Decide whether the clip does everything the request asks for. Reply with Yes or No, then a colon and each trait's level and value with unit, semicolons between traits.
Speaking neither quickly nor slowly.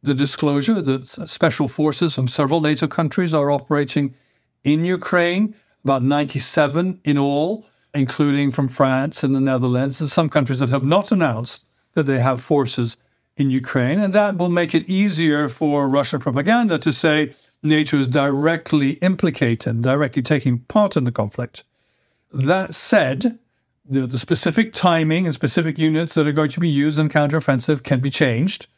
Yes: average, 160 wpm